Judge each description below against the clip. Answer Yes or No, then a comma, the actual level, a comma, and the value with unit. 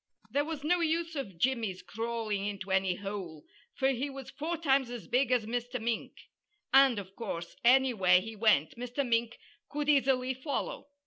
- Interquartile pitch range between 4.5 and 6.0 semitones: Yes, average, 4.8 semitones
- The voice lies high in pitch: Yes, high, 245 Hz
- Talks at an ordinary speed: Yes, average, 170 wpm